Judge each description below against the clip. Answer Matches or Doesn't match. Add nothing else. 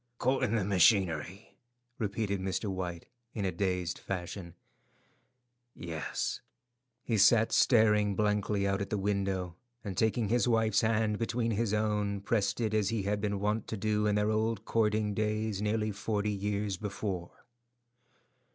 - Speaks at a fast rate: Doesn't match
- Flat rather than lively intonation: Matches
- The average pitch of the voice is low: Matches